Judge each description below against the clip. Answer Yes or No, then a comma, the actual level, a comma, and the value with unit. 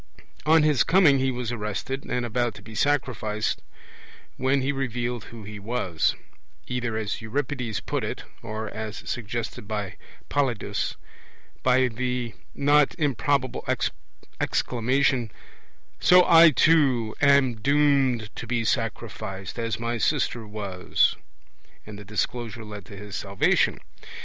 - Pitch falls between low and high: No, low, 120 Hz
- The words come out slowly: Yes, slow, 125 wpm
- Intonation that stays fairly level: No, average, 3.8 semitones